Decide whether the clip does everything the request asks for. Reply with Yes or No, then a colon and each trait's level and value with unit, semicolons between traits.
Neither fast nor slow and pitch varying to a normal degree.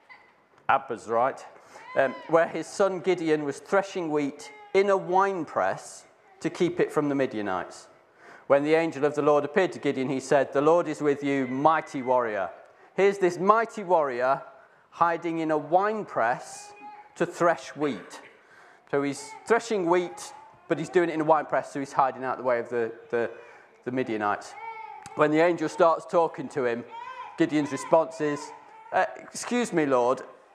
No: average, 165 wpm; wide, 6.4 semitones